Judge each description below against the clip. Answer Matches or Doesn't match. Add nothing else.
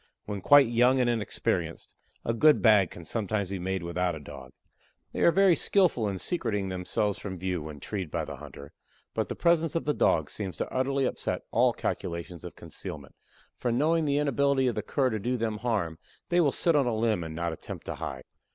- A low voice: Matches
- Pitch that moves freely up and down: Matches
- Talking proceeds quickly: Matches